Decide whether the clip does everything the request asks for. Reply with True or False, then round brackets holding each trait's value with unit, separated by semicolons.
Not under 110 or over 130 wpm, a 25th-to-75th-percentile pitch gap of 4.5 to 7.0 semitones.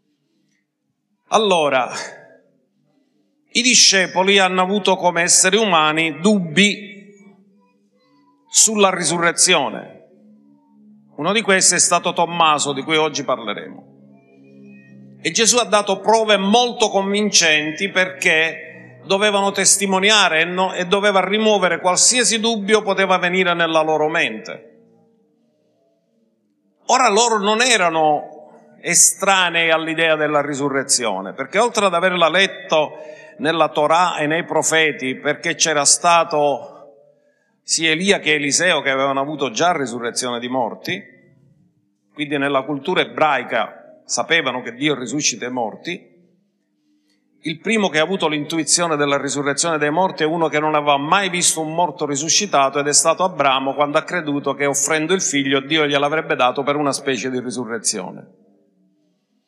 True (125 wpm; 5.2 semitones)